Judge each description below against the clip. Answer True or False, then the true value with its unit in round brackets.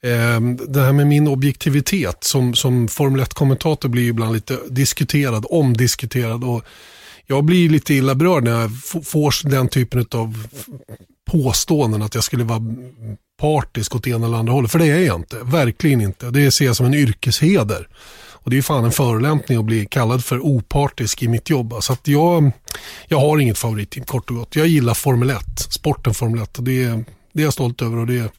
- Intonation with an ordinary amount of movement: True (3.6 semitones)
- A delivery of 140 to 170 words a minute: False (190 wpm)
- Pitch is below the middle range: True (125 Hz)